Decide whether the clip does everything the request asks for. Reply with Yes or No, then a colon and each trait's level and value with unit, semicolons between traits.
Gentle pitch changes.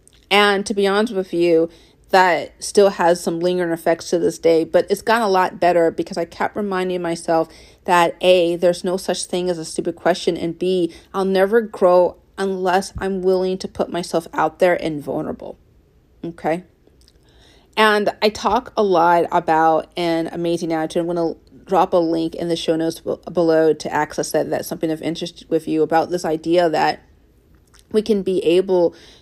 Yes: narrow, 2.1 semitones